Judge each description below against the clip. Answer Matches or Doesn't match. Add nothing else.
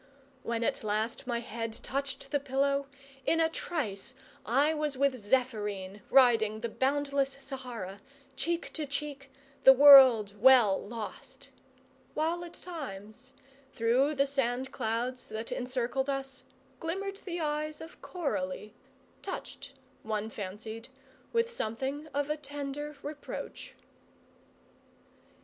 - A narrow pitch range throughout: Doesn't match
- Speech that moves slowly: Matches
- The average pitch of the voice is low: Doesn't match